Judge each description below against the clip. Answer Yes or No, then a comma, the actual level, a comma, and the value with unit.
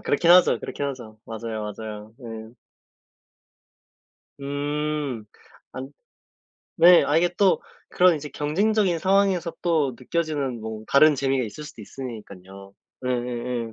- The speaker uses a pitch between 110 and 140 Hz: Yes, low, 135 Hz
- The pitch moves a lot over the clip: Yes, wide, 6.1 semitones